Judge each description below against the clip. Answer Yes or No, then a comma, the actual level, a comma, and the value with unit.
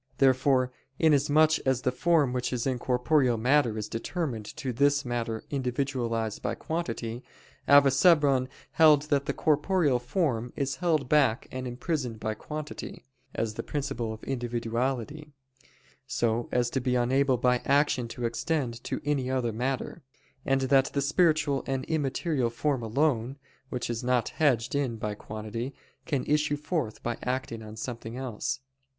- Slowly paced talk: No, average, 150 wpm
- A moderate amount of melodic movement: Yes, average, 3.4 semitones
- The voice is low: Yes, low, 130 Hz